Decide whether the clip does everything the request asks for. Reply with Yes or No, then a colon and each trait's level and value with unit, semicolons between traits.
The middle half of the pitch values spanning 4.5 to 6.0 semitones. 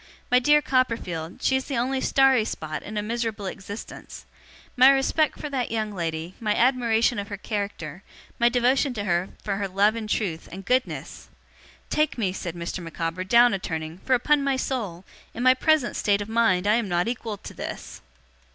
Yes: average, 5.1 semitones